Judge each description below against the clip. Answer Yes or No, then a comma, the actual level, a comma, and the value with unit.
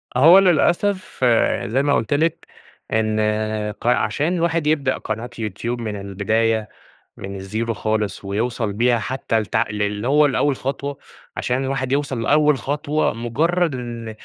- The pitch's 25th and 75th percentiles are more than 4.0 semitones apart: Yes, average, 4.8 semitones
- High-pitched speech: No, low, 125 Hz